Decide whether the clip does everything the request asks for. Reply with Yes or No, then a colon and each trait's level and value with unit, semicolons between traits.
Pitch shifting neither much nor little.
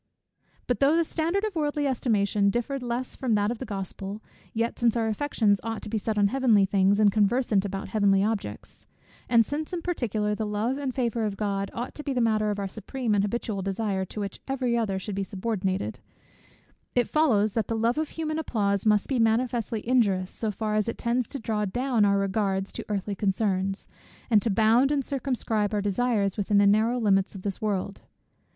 Yes: average, 3.4 semitones